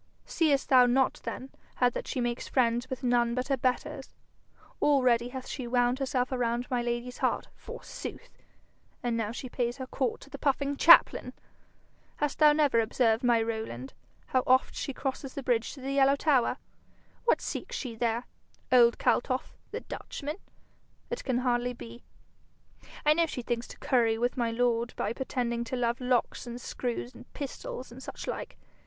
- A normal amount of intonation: No, narrow, 2.1 semitones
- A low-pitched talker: No, very high, 250 Hz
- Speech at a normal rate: Yes, average, 175 wpm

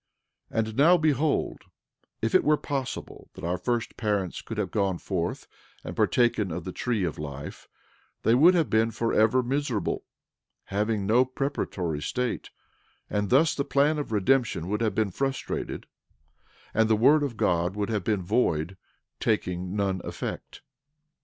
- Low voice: Yes, low, 110 Hz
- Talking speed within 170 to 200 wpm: No, average, 155 wpm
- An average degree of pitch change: No, wide, 5.8 semitones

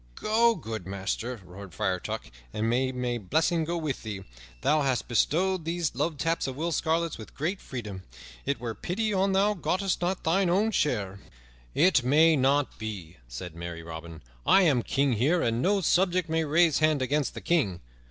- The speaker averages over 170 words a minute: Yes, average, 180 wpm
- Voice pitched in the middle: Yes, medium, 145 Hz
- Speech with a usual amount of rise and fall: No, wide, 7.6 semitones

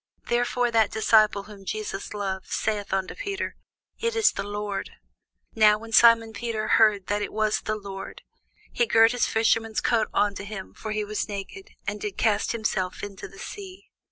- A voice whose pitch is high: Yes, high, 215 Hz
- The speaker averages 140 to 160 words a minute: No, average, 175 wpm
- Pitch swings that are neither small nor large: No, narrow, 2.0 semitones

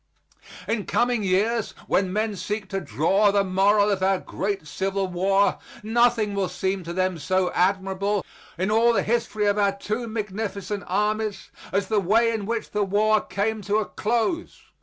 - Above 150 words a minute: Yes, average, 170 wpm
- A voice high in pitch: Yes, high, 200 Hz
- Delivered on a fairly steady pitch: Yes, narrow, 2.2 semitones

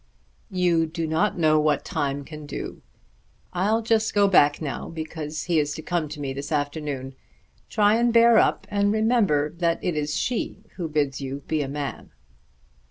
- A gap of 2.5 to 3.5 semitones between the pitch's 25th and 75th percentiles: No, wide, 5.4 semitones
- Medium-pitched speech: Yes, medium, 160 Hz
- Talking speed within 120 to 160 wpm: No, average, 175 wpm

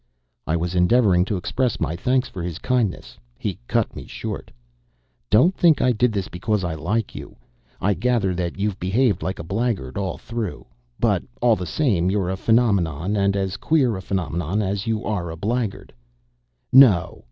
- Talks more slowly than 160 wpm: No, average, 175 wpm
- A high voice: No, low, 100 Hz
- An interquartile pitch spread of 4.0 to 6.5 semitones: Yes, average, 4.7 semitones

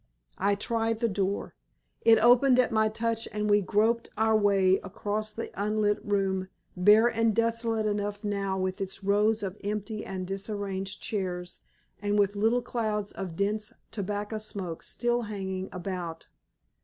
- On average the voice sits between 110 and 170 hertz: No, high, 205 Hz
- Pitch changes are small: Yes, narrow, 2.2 semitones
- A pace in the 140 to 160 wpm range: Yes, average, 150 wpm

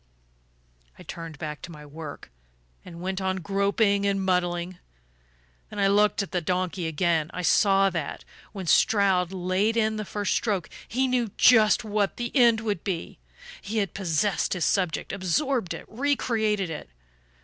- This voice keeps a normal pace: Yes, average, 160 wpm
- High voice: Yes, high, 195 Hz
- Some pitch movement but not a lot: Yes, average, 3.4 semitones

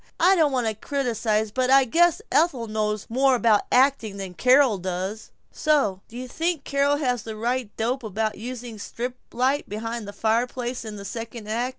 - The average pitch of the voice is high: Yes, high, 235 Hz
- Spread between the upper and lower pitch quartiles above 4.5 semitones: No, average, 3.6 semitones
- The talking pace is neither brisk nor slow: Yes, average, 190 wpm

